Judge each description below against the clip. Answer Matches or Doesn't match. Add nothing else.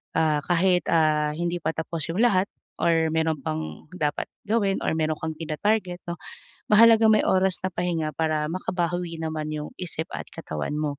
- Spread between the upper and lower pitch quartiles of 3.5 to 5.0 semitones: Doesn't match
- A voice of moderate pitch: Matches